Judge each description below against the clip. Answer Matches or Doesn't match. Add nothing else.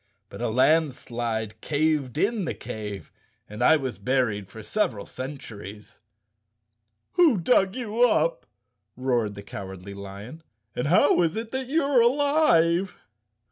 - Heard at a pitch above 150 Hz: Doesn't match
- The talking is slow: Matches